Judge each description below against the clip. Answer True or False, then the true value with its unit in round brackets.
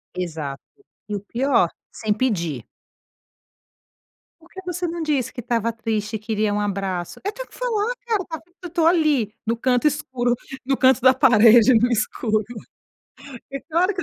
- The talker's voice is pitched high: True (245 Hz)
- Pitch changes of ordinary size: False (6.5 semitones)